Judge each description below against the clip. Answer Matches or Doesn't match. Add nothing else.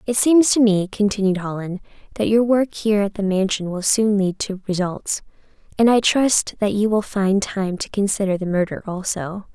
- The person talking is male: Doesn't match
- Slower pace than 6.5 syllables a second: Matches